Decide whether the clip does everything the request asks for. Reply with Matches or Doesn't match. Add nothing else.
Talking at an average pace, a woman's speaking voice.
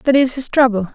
Doesn't match